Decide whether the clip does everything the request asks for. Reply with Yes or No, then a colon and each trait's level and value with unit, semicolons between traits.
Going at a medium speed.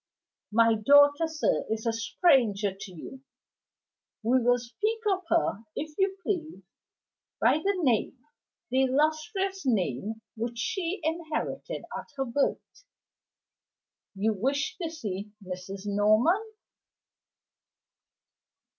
No: slow, 110 wpm